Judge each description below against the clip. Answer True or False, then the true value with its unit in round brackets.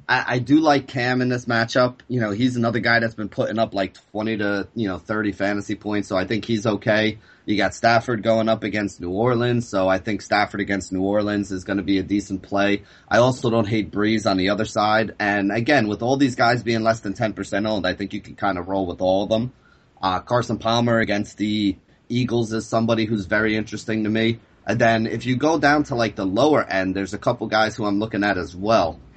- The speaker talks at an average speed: False (240 wpm)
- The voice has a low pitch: True (110 Hz)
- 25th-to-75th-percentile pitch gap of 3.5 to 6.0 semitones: False (2.5 semitones)